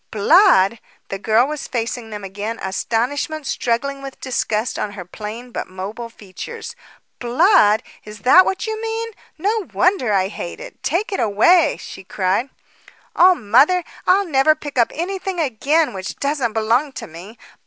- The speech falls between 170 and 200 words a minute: No, average, 155 wpm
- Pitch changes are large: Yes, wide, 7.9 semitones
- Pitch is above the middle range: Yes, high, 245 Hz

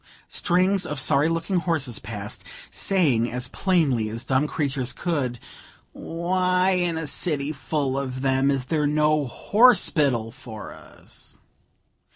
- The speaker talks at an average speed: No, slow, 130 wpm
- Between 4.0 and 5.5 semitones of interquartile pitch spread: Yes, average, 4.8 semitones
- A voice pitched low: No, medium, 145 Hz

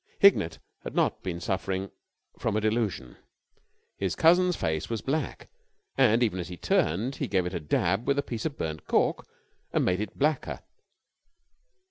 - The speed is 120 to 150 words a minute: No, average, 165 wpm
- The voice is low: Yes, low, 105 Hz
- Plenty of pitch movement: Yes, wide, 6.9 semitones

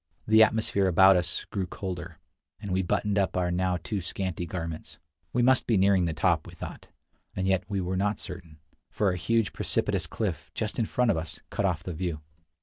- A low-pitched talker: Yes, very low, 95 Hz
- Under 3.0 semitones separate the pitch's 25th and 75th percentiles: Yes, narrow, 2.5 semitones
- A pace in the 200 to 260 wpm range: Yes, fast, 205 wpm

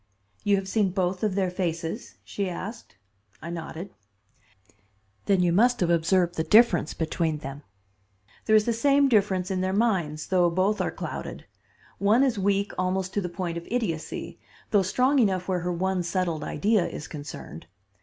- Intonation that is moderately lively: Yes, average, 3.2 semitones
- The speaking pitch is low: No, medium, 185 Hz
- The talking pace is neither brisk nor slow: Yes, average, 170 wpm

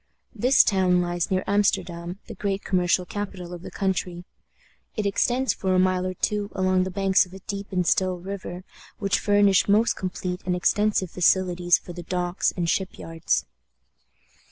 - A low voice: No, medium, 185 Hz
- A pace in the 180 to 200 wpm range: No, average, 170 wpm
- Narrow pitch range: Yes, narrow, 2.0 semitones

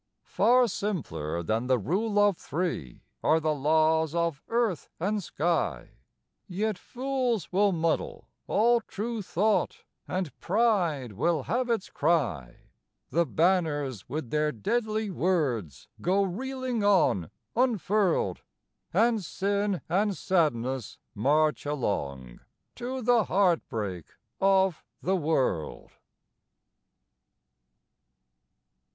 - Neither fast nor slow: No, slow, 100 wpm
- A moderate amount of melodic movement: No, wide, 7.0 semitones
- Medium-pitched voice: Yes, medium, 175 Hz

